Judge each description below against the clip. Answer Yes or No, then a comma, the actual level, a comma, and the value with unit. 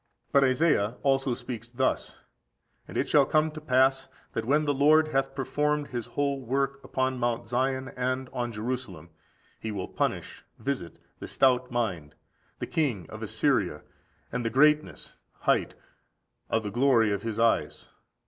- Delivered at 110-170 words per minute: Yes, average, 160 wpm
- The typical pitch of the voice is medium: No, low, 130 Hz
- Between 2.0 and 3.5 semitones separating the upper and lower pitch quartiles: Yes, average, 3.1 semitones